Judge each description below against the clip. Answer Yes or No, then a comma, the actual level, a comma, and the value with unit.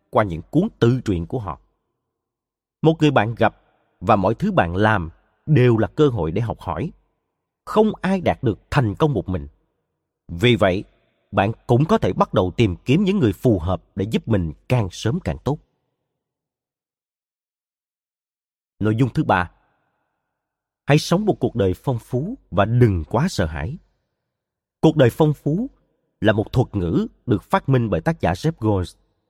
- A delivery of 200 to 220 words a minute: No, average, 170 wpm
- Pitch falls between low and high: No, low, 115 Hz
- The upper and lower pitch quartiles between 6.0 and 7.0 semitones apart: Yes, wide, 6.5 semitones